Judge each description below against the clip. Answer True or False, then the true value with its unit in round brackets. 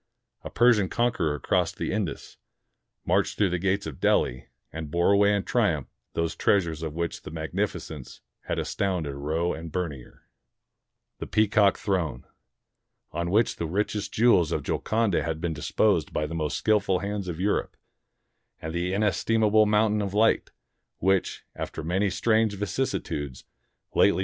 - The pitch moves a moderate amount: True (4.4 semitones)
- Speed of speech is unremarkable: True (150 wpm)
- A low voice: True (95 Hz)